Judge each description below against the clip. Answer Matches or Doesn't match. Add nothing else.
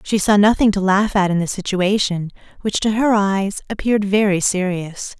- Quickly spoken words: Doesn't match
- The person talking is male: Doesn't match